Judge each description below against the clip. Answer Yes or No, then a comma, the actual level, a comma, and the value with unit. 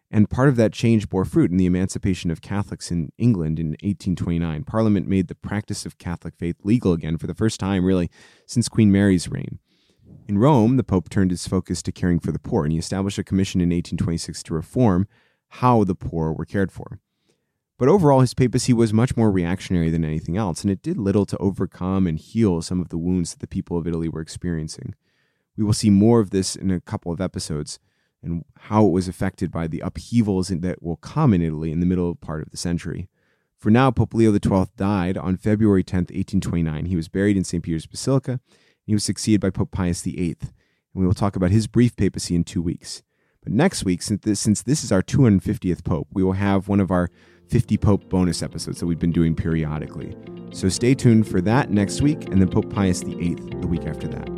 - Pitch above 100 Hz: No, very low, 95 Hz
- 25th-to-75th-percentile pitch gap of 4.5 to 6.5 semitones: No, average, 3.7 semitones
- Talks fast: Yes, fast, 225 wpm